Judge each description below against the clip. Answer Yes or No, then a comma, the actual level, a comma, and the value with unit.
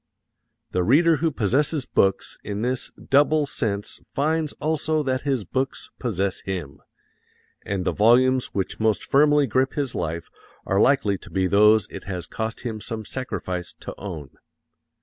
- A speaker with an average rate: Yes, average, 150 wpm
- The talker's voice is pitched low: Yes, low, 115 Hz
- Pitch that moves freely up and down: Yes, wide, 6.1 semitones